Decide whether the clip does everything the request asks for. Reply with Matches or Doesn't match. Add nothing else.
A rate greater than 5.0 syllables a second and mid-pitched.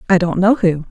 Matches